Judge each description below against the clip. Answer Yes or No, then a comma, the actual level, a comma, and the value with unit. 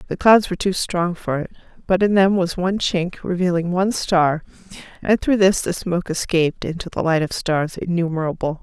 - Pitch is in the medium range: Yes, medium, 175 Hz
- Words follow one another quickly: No, average, 195 wpm